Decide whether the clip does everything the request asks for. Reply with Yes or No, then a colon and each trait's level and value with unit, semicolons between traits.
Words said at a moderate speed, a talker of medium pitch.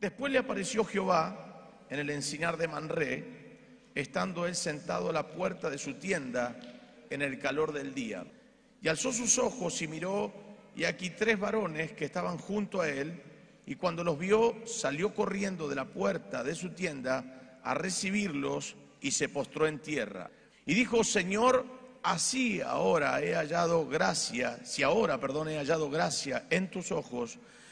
Yes: average, 160 wpm; medium, 180 Hz